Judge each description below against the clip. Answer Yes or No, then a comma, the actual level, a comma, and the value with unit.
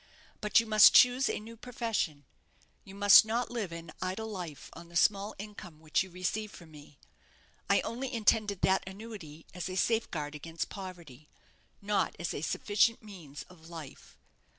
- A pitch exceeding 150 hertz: Yes, high, 190 Hz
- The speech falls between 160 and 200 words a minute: Yes, average, 165 wpm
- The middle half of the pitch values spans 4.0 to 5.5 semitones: Yes, average, 4.7 semitones